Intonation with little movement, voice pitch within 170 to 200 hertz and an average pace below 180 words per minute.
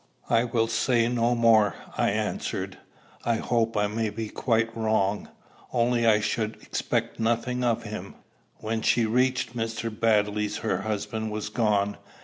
No: narrow, 1.6 semitones; low, 115 Hz; average, 145 wpm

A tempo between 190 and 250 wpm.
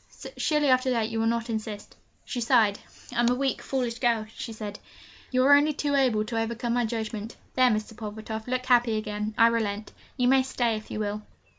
Yes: fast, 205 wpm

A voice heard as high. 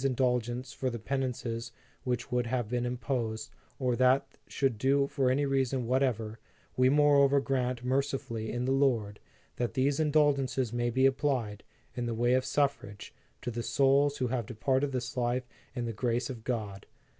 No: low, 125 Hz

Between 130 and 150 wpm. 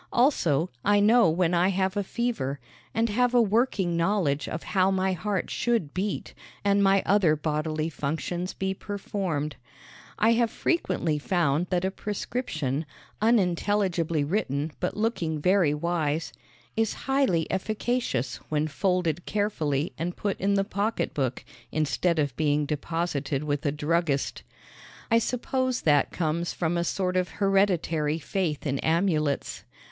Yes: average, 140 wpm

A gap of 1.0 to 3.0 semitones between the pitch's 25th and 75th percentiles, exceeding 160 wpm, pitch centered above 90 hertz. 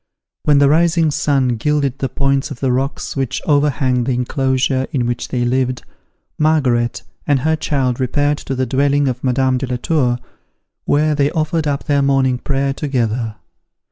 Yes: narrow, 2.4 semitones; average, 170 wpm; low, 135 Hz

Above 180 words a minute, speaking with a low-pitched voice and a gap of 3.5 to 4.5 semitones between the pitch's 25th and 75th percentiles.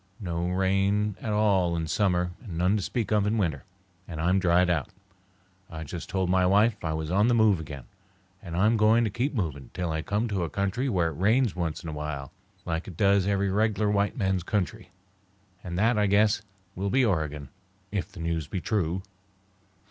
Yes: fast, 205 wpm; very low, 95 Hz; average, 3.8 semitones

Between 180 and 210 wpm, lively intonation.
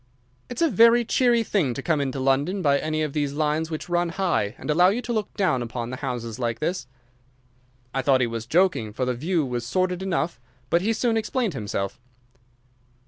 Yes: average, 200 wpm; wide, 6.8 semitones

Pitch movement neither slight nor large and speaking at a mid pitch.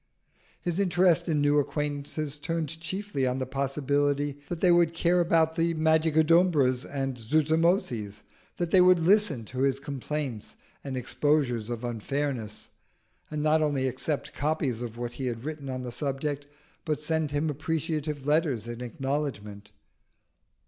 Yes: average, 3.6 semitones; medium, 145 Hz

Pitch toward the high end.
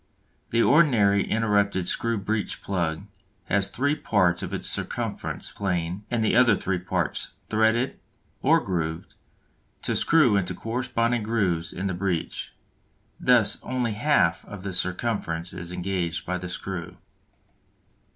No: low, 100 Hz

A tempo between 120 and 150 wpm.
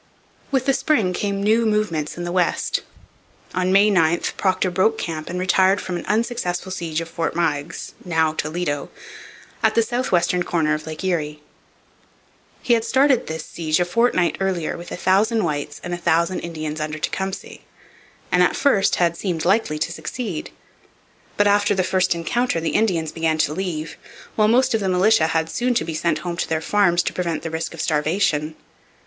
No: average, 185 wpm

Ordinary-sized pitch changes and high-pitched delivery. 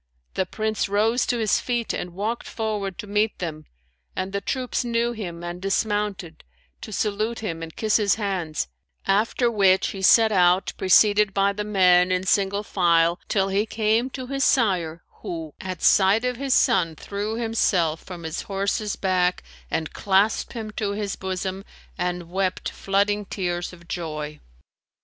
Yes: average, 3.2 semitones; high, 195 Hz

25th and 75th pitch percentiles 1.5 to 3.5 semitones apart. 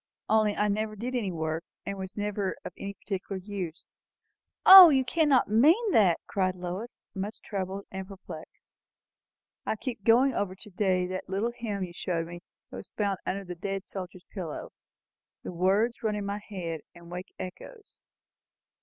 Yes: average, 2.9 semitones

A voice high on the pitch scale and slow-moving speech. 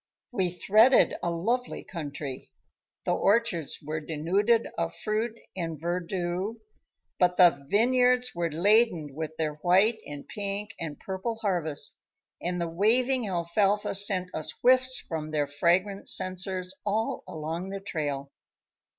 No: medium, 180 Hz; slow, 130 wpm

